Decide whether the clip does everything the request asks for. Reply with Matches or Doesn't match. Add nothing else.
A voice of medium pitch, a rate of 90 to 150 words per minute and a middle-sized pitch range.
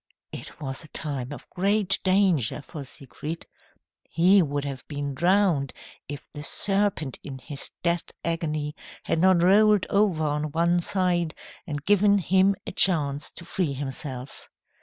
Matches